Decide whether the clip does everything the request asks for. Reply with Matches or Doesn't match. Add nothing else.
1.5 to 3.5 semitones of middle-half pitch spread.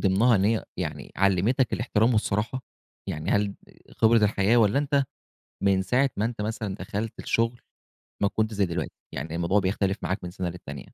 Matches